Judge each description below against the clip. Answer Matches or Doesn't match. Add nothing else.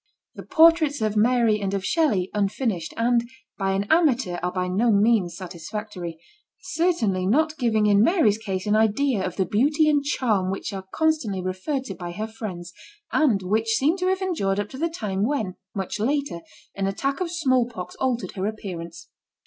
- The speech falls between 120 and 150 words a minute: Doesn't match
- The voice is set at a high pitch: Matches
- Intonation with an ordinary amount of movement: Doesn't match